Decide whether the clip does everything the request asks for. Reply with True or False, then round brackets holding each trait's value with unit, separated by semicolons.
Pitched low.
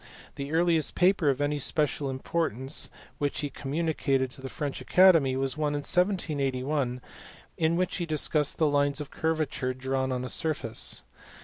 False (145 Hz)